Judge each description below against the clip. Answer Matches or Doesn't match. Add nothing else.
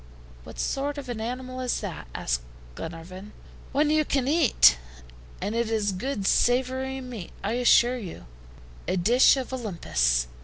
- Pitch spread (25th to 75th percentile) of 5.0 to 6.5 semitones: Matches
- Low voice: Doesn't match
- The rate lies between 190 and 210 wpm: Doesn't match